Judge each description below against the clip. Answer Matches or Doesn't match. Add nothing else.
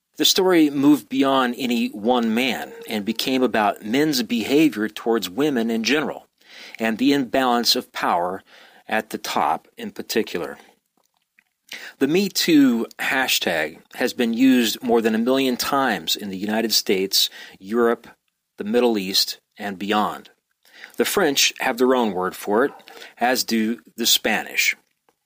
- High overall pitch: Doesn't match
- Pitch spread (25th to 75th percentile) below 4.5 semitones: Doesn't match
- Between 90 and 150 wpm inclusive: Matches